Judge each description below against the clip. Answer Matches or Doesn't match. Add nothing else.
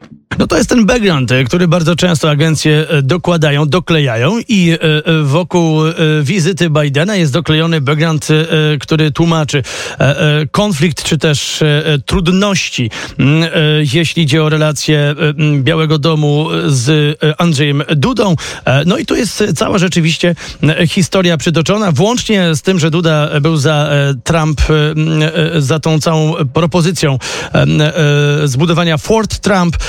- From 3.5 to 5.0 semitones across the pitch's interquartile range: Doesn't match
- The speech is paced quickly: Doesn't match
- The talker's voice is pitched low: Doesn't match